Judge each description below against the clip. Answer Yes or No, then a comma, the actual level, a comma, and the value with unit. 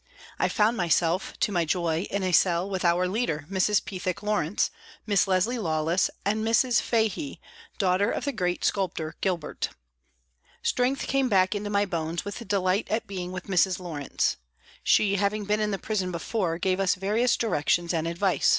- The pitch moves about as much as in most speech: Yes, average, 3.2 semitones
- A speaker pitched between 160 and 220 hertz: Yes, high, 190 Hz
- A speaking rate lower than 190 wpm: Yes, average, 170 wpm